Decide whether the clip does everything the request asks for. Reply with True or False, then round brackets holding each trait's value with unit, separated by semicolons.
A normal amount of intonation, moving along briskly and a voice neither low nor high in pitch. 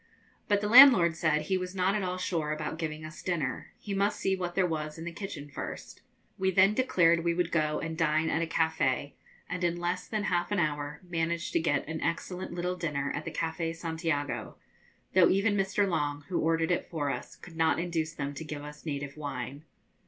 True (3.0 semitones; 210 wpm; 165 Hz)